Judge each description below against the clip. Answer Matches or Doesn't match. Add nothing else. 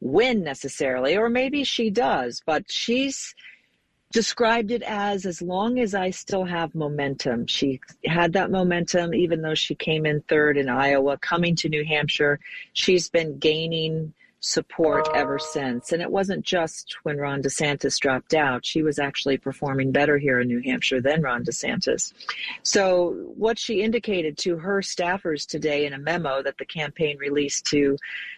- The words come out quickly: Doesn't match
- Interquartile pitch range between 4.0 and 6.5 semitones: Matches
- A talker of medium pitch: Matches